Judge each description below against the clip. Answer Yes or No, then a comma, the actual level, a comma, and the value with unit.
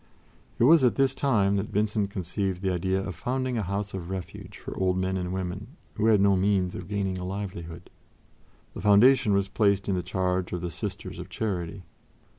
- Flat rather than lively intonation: Yes, narrow, 2.2 semitones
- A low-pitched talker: Yes, very low, 95 Hz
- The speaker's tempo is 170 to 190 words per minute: No, average, 200 wpm